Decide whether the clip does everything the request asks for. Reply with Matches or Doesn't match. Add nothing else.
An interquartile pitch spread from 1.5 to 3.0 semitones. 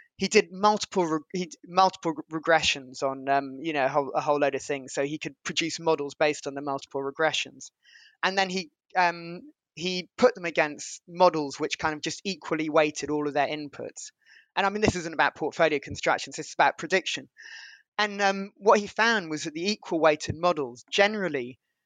Doesn't match